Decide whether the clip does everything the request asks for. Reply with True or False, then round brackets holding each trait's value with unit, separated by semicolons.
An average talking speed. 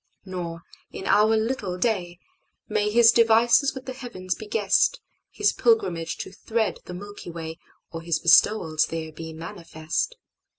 False (130 wpm)